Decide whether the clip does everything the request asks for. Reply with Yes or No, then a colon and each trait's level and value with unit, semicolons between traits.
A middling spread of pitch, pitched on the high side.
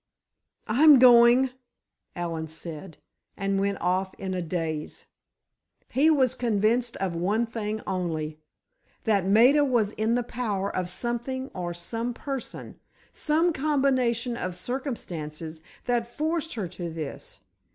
No: wide, 5.9 semitones; high, 220 Hz